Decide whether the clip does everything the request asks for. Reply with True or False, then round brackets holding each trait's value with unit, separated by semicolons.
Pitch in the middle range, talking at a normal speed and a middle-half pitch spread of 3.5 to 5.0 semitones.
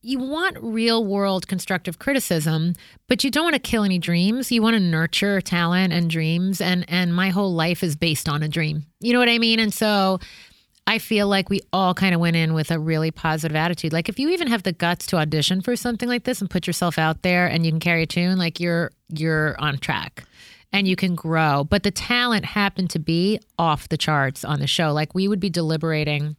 False (180 Hz; 230 wpm; 4.0 semitones)